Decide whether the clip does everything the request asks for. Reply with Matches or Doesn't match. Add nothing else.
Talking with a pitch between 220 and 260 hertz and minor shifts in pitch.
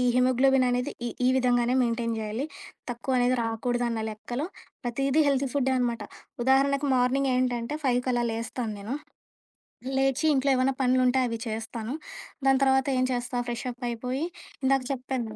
Matches